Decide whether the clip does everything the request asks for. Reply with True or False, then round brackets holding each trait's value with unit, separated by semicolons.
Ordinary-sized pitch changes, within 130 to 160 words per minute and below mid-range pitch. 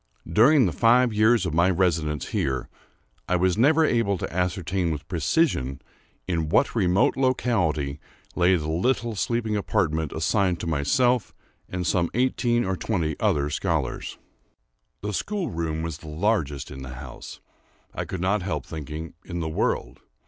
False (5.8 semitones; 150 wpm; 90 Hz)